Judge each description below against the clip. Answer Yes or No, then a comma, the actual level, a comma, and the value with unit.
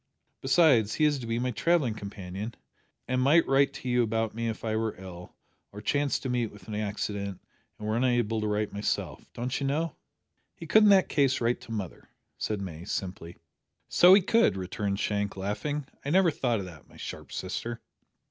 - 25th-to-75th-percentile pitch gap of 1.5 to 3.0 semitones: No, average, 5.0 semitones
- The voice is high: No, low, 115 Hz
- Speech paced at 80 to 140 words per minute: No, average, 195 wpm